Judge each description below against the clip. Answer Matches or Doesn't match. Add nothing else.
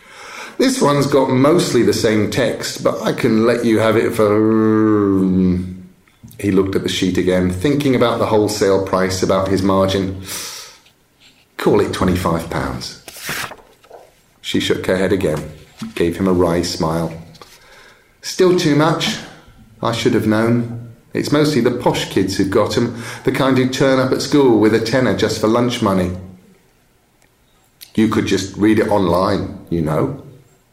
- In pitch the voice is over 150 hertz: Doesn't match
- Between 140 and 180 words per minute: Matches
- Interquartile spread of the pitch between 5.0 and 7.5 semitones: Matches